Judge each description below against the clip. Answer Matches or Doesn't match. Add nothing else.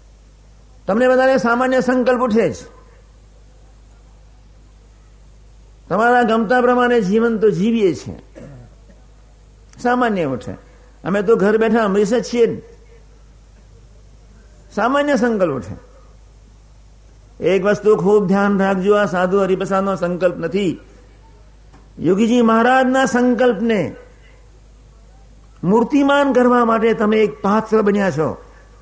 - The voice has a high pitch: Matches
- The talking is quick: Doesn't match